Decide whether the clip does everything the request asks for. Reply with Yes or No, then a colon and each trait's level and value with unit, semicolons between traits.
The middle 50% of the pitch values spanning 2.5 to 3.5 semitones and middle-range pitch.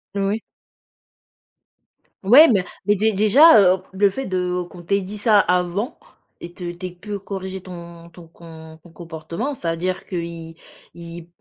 Yes: average, 2.9 semitones; medium, 180 Hz